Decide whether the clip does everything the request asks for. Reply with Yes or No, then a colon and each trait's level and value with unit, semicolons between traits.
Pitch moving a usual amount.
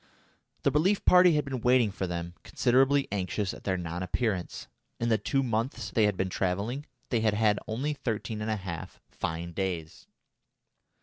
No: wide, 5.7 semitones